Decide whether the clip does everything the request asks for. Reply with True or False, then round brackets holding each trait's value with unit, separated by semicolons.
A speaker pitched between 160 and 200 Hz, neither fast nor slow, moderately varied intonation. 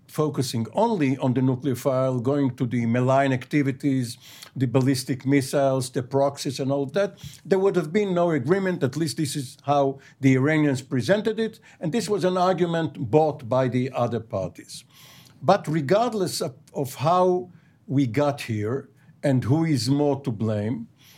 False (140 Hz; 160 wpm; 3.4 semitones)